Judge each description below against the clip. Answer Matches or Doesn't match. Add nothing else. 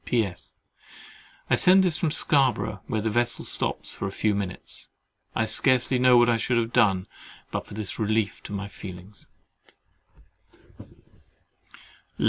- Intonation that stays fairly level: Doesn't match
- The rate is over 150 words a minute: Doesn't match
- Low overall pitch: Matches